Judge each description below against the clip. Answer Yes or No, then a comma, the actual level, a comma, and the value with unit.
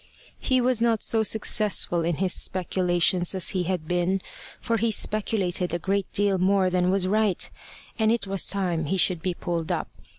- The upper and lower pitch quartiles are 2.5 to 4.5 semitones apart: Yes, average, 2.9 semitones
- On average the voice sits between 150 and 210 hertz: Yes, high, 190 Hz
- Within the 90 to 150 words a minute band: No, average, 185 wpm